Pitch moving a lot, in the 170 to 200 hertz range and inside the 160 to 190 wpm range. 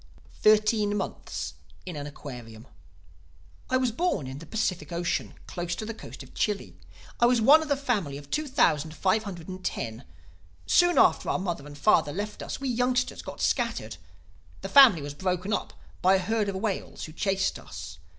Yes: wide, 7.2 semitones; high, 190 Hz; average, 180 wpm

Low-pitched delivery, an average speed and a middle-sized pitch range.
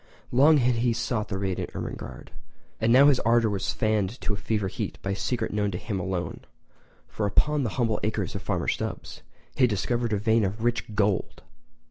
Yes: low, 110 Hz; average, 190 wpm; average, 3.0 semitones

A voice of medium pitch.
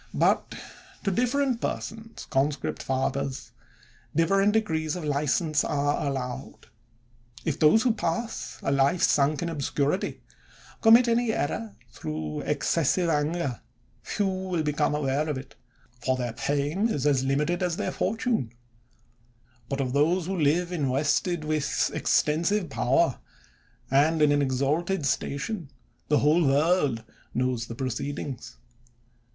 Yes: medium, 150 Hz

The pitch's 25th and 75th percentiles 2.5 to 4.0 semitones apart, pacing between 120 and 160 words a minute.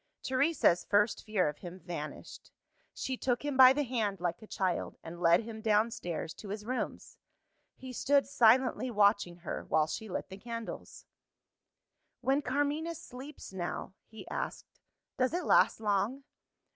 No: wide, 5.5 semitones; average, 150 wpm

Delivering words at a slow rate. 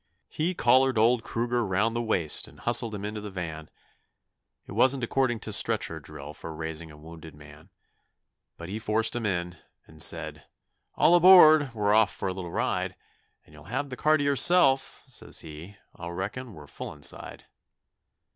No: average, 175 wpm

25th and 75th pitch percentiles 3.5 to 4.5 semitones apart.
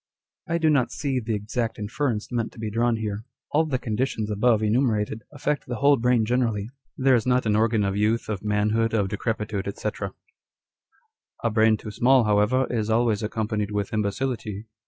No: average, 2.8 semitones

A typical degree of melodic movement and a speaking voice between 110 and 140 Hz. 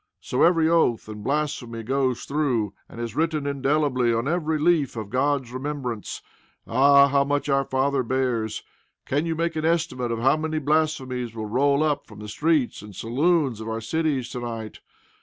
Yes: average, 4.4 semitones; low, 135 Hz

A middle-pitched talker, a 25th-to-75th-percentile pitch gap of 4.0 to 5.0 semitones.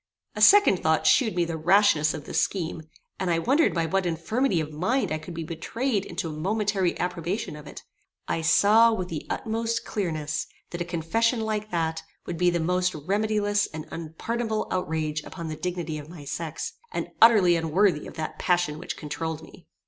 Yes: medium, 175 Hz; average, 4.5 semitones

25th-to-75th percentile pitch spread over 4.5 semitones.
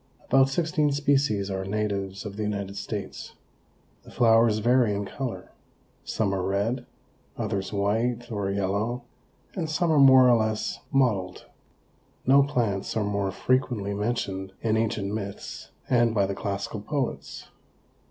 No: average, 3.9 semitones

